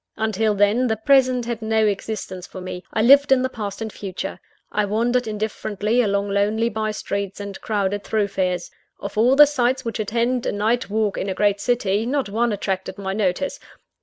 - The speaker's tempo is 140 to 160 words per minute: No, average, 190 wpm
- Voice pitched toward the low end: No, high, 215 Hz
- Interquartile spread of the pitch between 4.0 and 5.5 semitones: No, average, 2.9 semitones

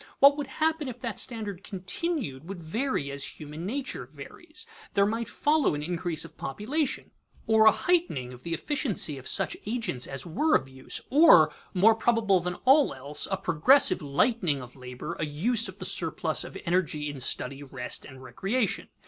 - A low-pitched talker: No, medium, 185 Hz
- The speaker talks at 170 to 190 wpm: Yes, average, 175 wpm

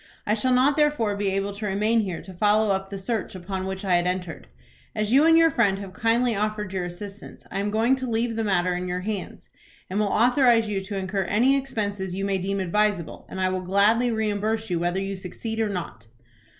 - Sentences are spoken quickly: Yes, fast, 225 wpm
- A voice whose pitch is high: Yes, high, 205 Hz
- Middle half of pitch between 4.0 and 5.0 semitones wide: No, average, 2.9 semitones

